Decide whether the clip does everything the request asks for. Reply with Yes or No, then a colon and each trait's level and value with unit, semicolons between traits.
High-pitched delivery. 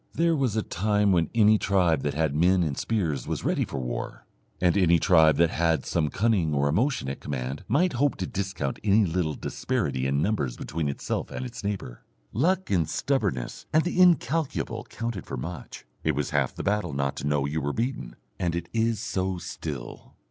No: very low, 90 Hz